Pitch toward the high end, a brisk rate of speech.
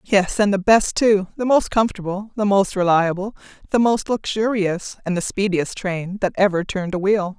No: high, 195 Hz; average, 180 wpm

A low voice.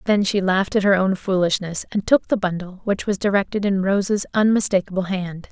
No: high, 195 Hz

